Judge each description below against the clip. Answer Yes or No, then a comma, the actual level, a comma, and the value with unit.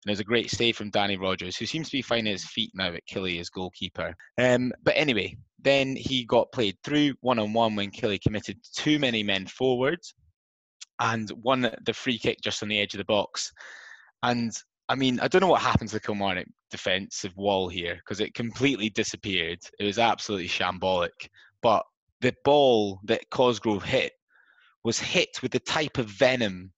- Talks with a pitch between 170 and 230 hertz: No, low, 115 Hz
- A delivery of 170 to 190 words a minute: Yes, average, 185 wpm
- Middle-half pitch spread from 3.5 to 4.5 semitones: Yes, average, 4.2 semitones